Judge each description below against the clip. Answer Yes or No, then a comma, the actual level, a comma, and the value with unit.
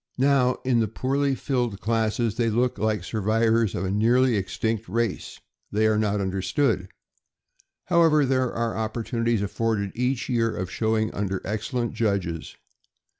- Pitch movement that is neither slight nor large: Yes, average, 3.1 semitones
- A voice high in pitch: No, low, 115 Hz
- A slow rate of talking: No, average, 145 wpm